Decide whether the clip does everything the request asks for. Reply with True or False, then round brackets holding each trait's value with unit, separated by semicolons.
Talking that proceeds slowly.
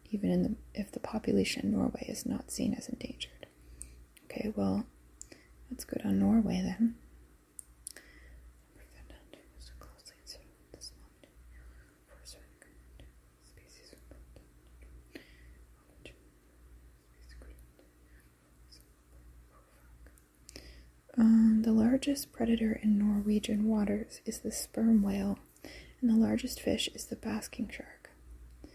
True (80 wpm)